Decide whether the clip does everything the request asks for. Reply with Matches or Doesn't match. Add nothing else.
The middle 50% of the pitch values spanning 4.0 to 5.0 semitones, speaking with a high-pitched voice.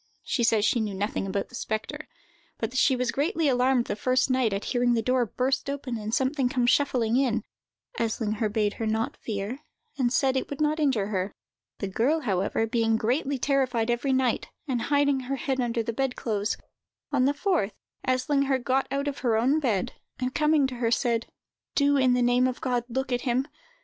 Doesn't match